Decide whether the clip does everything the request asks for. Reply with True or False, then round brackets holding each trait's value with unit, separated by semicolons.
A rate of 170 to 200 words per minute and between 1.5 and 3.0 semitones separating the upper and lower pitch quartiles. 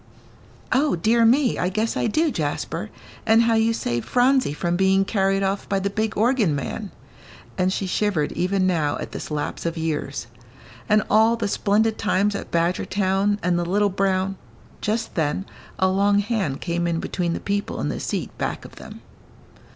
False (180 wpm; 3.7 semitones)